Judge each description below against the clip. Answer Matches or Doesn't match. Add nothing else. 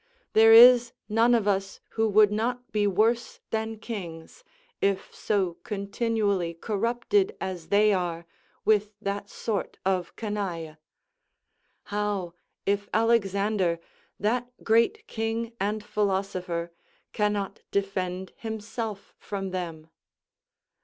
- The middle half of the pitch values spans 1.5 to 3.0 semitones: Matches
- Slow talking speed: Matches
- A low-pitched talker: Doesn't match